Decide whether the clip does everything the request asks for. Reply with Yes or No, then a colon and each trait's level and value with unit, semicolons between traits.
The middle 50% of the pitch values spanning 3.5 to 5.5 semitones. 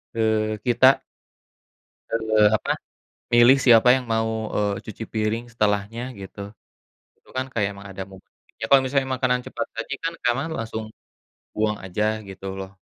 No: average, 2.7 semitones